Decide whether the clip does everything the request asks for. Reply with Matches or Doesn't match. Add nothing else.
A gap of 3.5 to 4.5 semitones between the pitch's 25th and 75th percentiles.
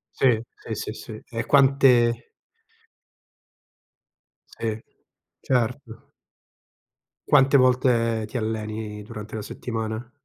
Doesn't match